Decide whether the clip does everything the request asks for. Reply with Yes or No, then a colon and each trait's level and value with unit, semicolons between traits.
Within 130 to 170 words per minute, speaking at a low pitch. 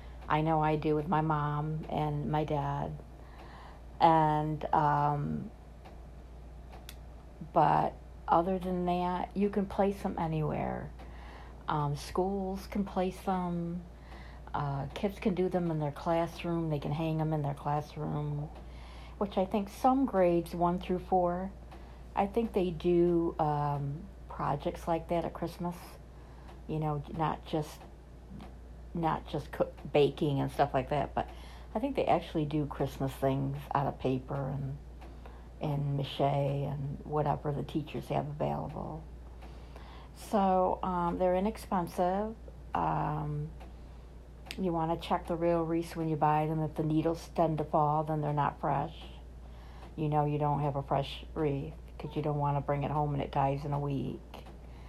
No: average, 150 wpm; medium, 150 Hz